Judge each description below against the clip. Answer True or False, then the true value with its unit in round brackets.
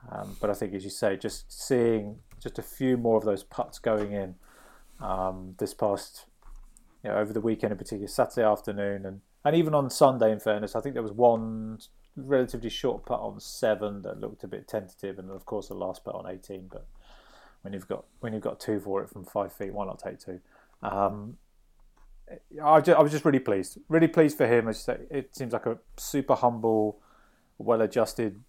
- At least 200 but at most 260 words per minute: True (205 wpm)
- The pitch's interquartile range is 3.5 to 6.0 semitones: True (4.1 semitones)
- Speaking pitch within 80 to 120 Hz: True (110 Hz)